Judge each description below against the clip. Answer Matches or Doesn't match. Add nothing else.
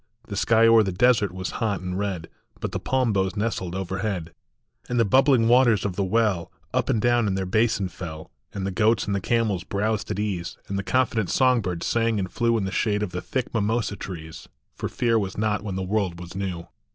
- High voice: Doesn't match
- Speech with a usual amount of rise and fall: Matches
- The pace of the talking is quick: Matches